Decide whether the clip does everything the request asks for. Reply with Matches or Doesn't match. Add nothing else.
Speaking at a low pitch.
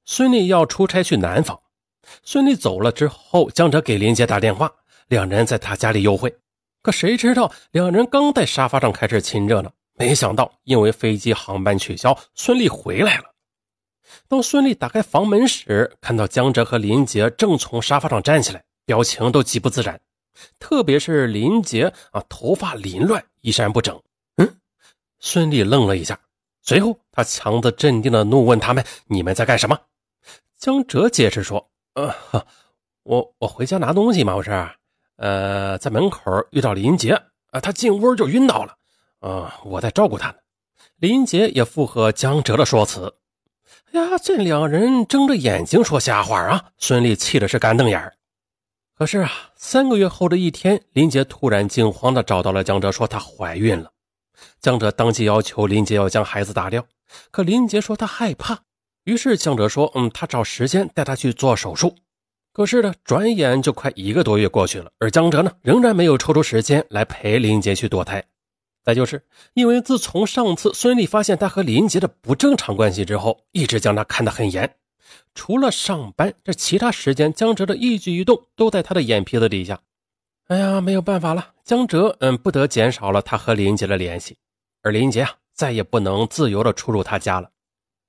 Matches